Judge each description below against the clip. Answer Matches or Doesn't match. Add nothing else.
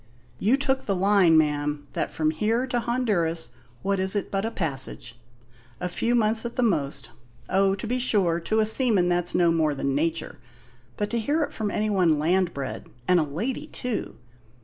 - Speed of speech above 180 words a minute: Matches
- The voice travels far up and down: Matches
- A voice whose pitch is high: Matches